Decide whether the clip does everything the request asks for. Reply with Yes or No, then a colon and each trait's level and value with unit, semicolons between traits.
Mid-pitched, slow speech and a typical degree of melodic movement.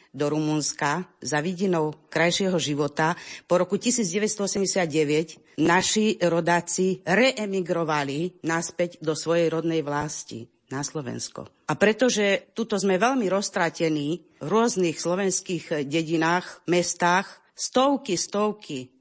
Yes: medium, 175 Hz; slow, 100 wpm; average, 3.7 semitones